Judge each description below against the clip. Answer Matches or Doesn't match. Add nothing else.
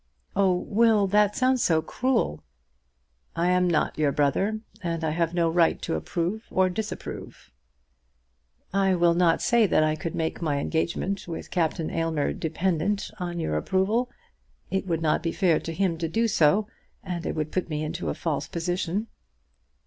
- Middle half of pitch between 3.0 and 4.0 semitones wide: Matches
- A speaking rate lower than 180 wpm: Matches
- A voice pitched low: Doesn't match